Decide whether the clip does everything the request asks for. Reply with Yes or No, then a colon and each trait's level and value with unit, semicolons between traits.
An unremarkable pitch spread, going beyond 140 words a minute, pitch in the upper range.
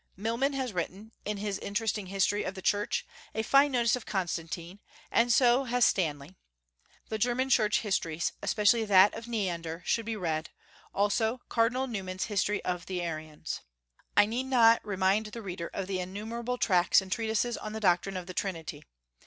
Yes: average, 3.9 semitones; average, 170 wpm; high, 205 Hz